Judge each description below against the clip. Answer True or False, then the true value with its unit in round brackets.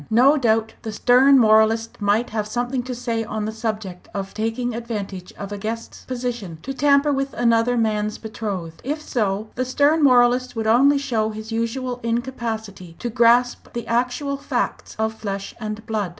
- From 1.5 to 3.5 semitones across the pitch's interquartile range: True (2.5 semitones)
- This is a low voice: False (230 Hz)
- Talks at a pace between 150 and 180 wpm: True (170 wpm)